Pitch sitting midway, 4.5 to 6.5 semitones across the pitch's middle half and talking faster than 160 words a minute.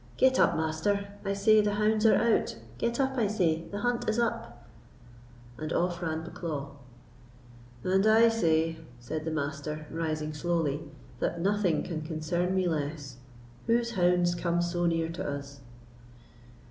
No: medium, 175 Hz; average, 4.8 semitones; average, 145 wpm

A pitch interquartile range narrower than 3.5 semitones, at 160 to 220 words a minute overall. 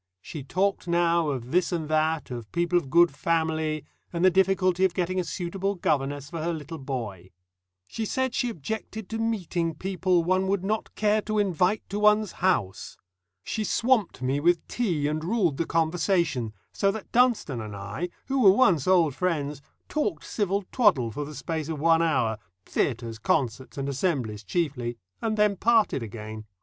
No: wide, 5.6 semitones; average, 175 wpm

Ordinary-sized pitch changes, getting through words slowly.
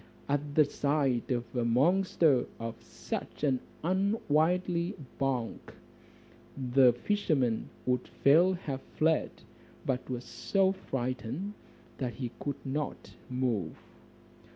Yes: average, 4.7 semitones; slow, 105 wpm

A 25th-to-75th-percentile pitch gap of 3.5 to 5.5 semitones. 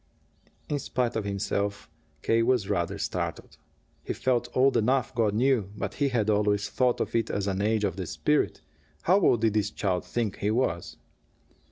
Yes: average, 3.8 semitones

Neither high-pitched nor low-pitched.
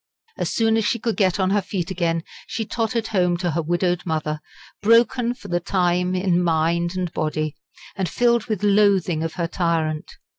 Yes: medium, 180 Hz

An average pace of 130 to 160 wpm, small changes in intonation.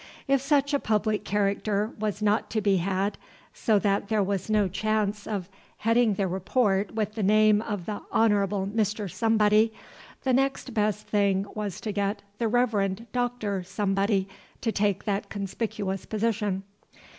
Yes: average, 155 wpm; narrow, 1.8 semitones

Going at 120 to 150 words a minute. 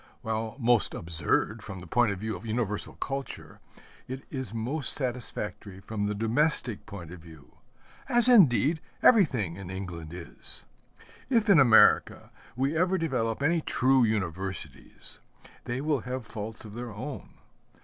Yes: average, 145 wpm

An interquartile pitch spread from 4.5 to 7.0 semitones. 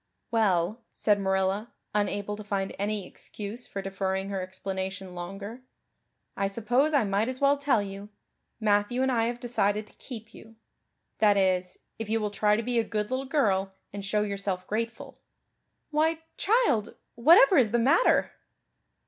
No: average, 3.4 semitones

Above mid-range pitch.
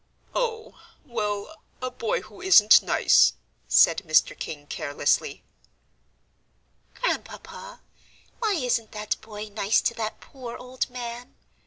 Yes: high, 230 Hz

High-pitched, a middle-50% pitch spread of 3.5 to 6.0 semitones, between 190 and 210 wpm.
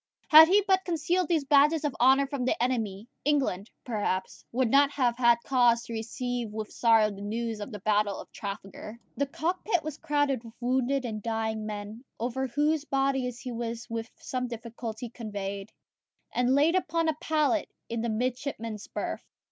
No: high, 245 Hz; average, 4.2 semitones; average, 170 wpm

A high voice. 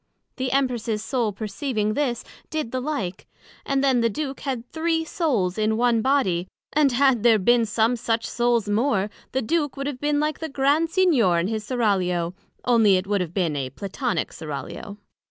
Yes: high, 235 Hz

